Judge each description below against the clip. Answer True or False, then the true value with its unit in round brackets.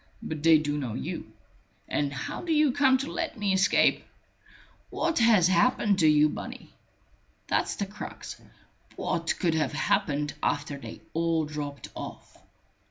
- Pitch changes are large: True (6.1 semitones)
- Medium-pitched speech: True (165 Hz)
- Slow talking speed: False (150 wpm)